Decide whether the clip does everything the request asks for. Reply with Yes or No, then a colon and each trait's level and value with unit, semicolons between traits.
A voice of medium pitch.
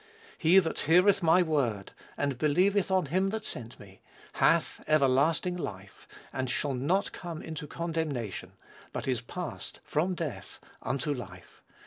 Yes: medium, 155 Hz